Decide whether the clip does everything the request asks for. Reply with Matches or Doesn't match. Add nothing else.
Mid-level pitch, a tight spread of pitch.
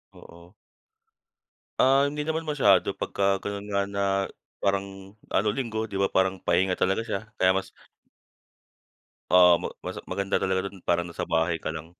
Doesn't match